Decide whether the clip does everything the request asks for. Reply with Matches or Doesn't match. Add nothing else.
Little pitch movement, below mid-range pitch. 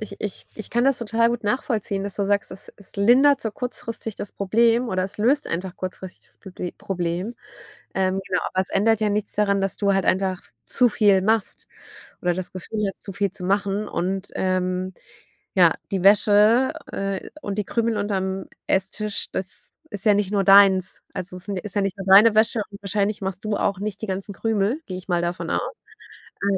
Doesn't match